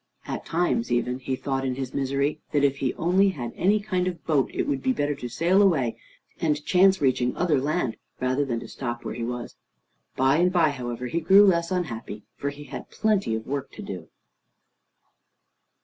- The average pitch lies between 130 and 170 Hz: Yes, medium, 140 Hz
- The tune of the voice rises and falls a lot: Yes, wide, 5.8 semitones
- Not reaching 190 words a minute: No, average, 200 wpm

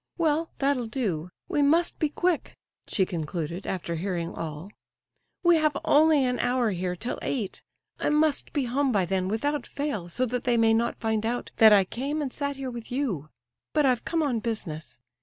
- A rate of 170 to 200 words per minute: Yes, average, 190 wpm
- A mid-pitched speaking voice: No, high, 240 Hz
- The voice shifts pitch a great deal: Yes, wide, 7.2 semitones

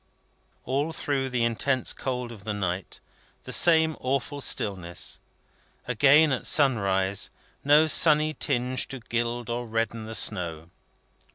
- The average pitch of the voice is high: No, low, 120 Hz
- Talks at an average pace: No, slow, 125 wpm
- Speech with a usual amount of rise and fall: Yes, average, 4.6 semitones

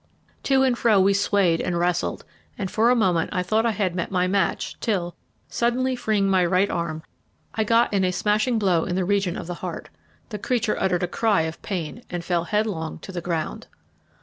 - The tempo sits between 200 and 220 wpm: Yes, fast, 205 wpm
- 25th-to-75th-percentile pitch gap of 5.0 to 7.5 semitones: No, average, 3.6 semitones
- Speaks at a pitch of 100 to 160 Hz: No, high, 190 Hz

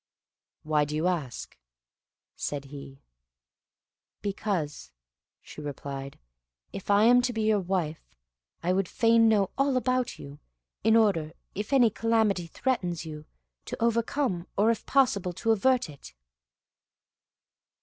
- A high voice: Yes, high, 195 Hz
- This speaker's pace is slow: Yes, slow, 130 wpm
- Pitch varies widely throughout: Yes, wide, 6.8 semitones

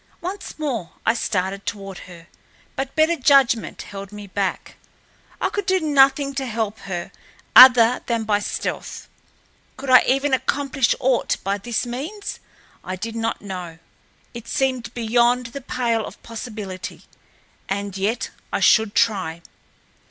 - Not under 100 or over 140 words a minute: Yes, slow, 135 wpm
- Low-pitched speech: No, high, 230 Hz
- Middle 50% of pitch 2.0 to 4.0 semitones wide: No, average, 4.9 semitones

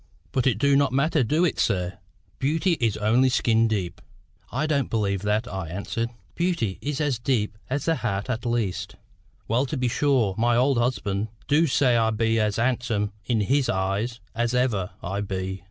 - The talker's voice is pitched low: Yes, low, 115 Hz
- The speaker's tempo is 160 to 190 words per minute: Yes, average, 185 wpm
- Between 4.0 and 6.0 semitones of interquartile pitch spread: Yes, average, 4.4 semitones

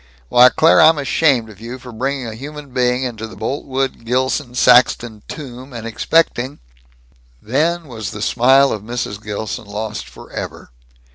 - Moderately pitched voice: No, low, 125 Hz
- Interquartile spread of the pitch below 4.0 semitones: Yes, average, 3.5 semitones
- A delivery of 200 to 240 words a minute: No, average, 155 wpm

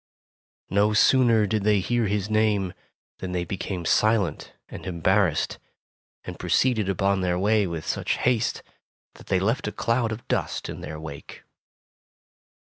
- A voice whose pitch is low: Yes, low, 100 Hz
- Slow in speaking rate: No, average, 150 wpm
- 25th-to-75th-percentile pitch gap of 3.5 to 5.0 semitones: No, average, 3.1 semitones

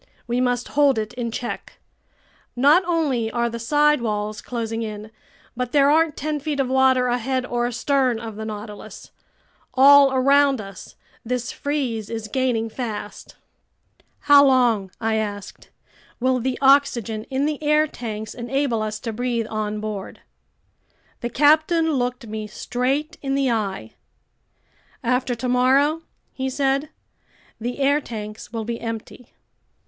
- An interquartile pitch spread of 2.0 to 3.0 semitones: No, average, 3.8 semitones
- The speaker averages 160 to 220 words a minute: No, average, 140 wpm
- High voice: Yes, high, 245 Hz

